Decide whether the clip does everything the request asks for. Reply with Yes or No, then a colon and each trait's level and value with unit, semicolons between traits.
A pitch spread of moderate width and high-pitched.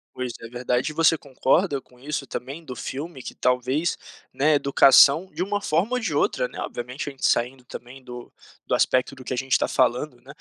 No: average, 3.4 semitones; low, 135 Hz